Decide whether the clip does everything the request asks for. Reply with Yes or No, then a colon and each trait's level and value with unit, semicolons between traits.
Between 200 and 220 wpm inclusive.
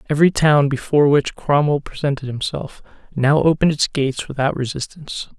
No: average, 145 wpm